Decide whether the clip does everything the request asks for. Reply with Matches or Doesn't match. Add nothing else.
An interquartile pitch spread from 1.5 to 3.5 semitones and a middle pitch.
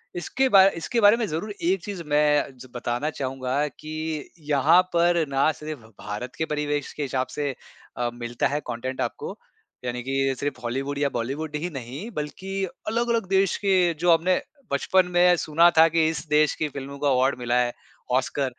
Doesn't match